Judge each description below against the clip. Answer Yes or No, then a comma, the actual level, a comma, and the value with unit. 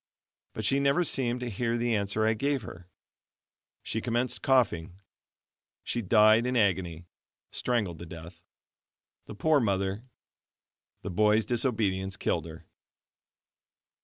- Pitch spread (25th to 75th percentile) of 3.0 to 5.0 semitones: Yes, average, 4.5 semitones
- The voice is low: Yes, low, 110 Hz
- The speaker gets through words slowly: Yes, slow, 125 wpm